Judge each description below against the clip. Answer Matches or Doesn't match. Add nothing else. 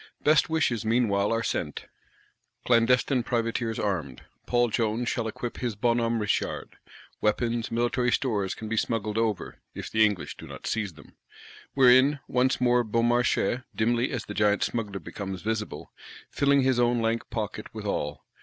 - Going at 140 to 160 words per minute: Matches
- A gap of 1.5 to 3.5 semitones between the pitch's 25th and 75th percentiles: Matches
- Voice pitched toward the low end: Matches